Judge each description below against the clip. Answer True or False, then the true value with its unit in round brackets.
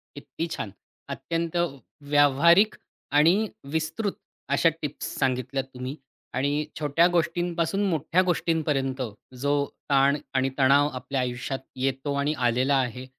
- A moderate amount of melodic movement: True (3.8 semitones)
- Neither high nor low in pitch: True (145 Hz)